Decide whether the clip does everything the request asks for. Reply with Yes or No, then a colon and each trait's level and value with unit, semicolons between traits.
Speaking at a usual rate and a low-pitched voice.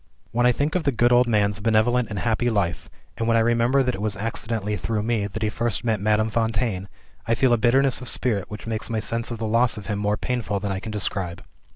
No: fast, 250 wpm; low, 110 Hz